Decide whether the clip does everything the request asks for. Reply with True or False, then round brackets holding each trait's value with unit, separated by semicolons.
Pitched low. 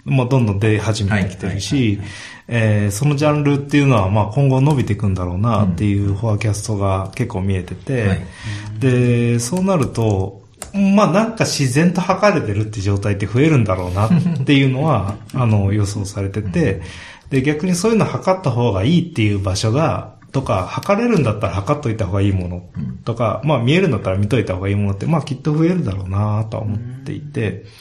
True (110 Hz)